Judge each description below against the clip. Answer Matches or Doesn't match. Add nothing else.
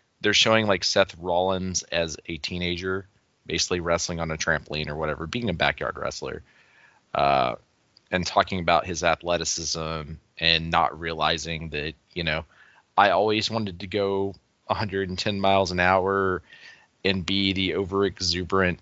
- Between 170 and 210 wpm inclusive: Doesn't match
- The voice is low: Matches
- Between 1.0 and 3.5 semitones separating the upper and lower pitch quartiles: Matches